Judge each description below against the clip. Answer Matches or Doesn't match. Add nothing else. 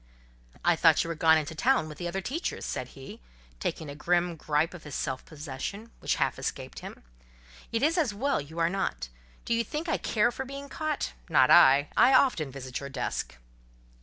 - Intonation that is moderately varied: Doesn't match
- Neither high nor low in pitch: Matches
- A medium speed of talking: Matches